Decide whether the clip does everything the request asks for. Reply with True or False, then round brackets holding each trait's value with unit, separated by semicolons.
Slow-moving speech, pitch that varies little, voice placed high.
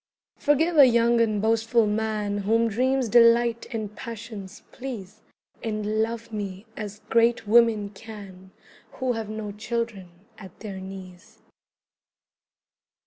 True (120 wpm; 2.2 semitones; 220 Hz)